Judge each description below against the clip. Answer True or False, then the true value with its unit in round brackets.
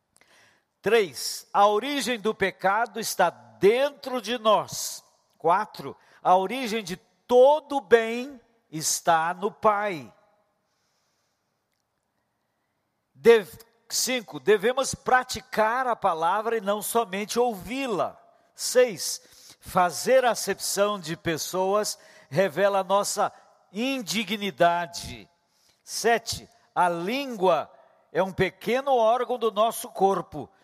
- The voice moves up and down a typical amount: True (4.3 semitones)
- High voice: True (215 Hz)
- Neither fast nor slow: False (95 wpm)